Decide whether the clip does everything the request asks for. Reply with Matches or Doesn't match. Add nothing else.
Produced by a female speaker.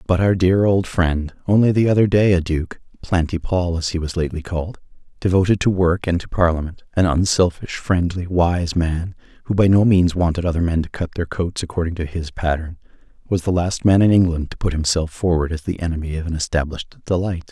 Doesn't match